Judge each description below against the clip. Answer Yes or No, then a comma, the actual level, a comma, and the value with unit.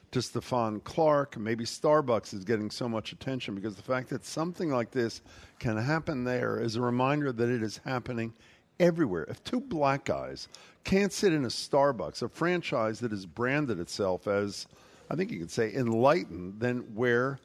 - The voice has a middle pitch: No, low, 120 Hz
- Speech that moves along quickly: No, average, 180 wpm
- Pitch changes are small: No, average, 4.0 semitones